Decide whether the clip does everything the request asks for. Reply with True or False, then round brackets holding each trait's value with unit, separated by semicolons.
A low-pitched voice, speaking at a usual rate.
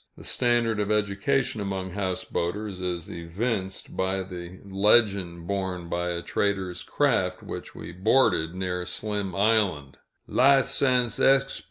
False (95 Hz; 125 wpm)